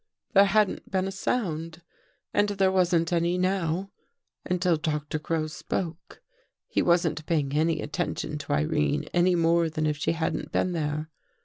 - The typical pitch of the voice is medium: Yes, medium, 170 Hz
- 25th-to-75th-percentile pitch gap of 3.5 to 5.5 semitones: No, average, 2.8 semitones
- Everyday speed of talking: Yes, average, 150 wpm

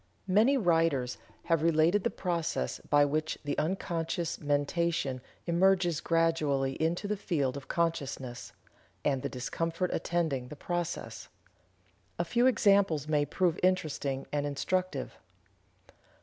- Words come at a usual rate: No, slow, 120 wpm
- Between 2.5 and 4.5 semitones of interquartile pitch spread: Yes, average, 3.5 semitones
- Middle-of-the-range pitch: Yes, medium, 165 Hz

